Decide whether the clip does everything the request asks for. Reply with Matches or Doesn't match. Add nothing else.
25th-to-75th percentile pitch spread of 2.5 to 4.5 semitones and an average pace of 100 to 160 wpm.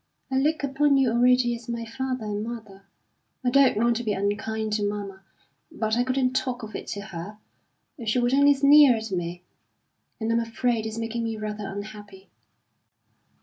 Doesn't match